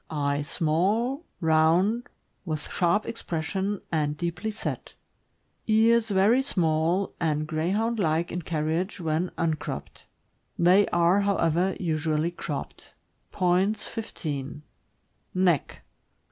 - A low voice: No, medium, 175 Hz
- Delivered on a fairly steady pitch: No, average, 4.2 semitones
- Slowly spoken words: Yes, slow, 105 wpm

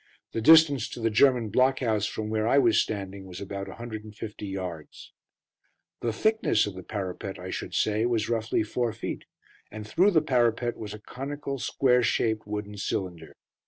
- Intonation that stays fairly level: No, average, 3.2 semitones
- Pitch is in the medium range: No, low, 110 Hz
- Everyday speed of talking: Yes, average, 170 wpm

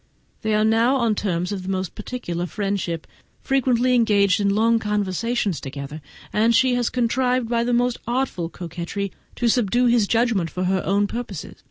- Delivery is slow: No, average, 170 wpm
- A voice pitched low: No, high, 215 Hz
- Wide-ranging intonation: No, average, 4.3 semitones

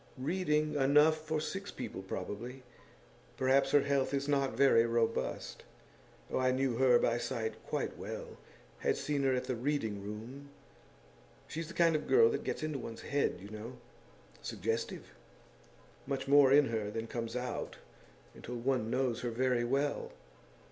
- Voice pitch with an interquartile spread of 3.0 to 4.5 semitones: Yes, average, 3.6 semitones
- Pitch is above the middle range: No, low, 130 Hz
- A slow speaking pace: No, average, 155 wpm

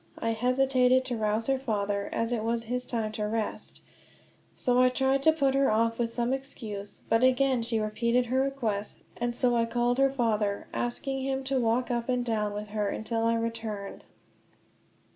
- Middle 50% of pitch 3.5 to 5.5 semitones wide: No, average, 2.8 semitones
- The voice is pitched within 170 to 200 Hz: No, high, 235 Hz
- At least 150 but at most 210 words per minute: Yes, average, 185 wpm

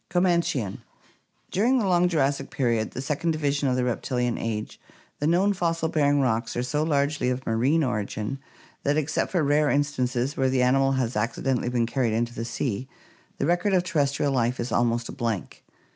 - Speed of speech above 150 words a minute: Yes, average, 185 wpm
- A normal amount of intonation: Yes, average, 4.2 semitones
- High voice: No, low, 135 Hz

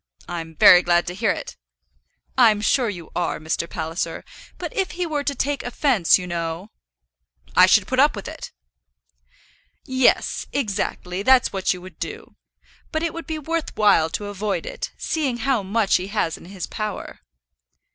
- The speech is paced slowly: No, average, 170 wpm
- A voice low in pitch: No, high, 210 Hz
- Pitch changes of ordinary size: No, wide, 7.5 semitones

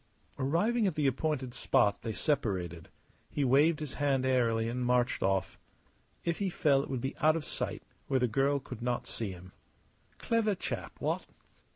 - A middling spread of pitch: Yes, average, 4.5 semitones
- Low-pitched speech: Yes, low, 130 Hz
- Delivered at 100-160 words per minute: No, average, 175 wpm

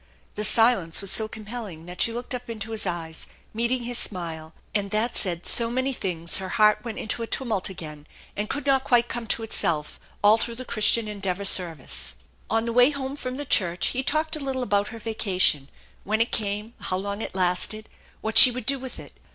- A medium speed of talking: No, fast, 210 wpm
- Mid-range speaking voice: No, high, 215 Hz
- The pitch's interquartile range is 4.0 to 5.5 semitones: Yes, average, 4.3 semitones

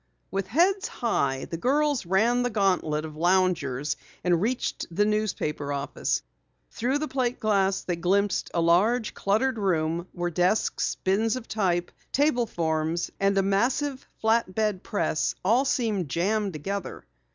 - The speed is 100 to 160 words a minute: Yes, average, 145 wpm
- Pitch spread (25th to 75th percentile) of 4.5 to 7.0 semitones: Yes, average, 5.1 semitones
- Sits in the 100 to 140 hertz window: No, high, 195 Hz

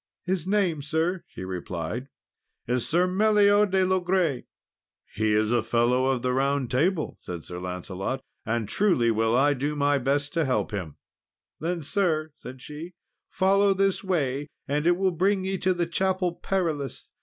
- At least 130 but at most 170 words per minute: Yes, average, 165 wpm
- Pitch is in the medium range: Yes, medium, 150 Hz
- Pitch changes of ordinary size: No, wide, 7.0 semitones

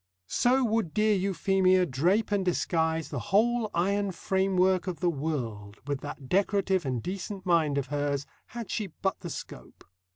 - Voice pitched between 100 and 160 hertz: No, medium, 185 Hz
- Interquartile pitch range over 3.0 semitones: Yes, average, 4.8 semitones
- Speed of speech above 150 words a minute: Yes, average, 160 wpm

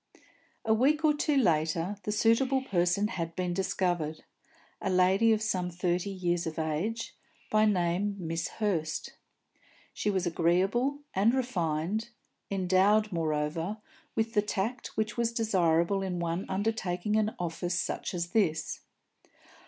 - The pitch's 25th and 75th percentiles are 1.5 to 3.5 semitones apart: No, average, 4.0 semitones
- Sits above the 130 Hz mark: Yes, high, 190 Hz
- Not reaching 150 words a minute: Yes, slow, 135 wpm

